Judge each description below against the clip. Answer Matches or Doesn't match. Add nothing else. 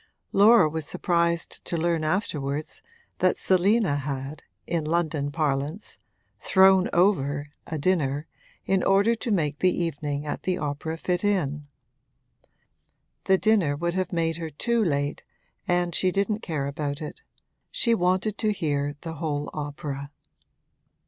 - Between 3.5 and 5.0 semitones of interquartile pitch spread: Matches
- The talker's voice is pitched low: Doesn't match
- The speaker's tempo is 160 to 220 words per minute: Doesn't match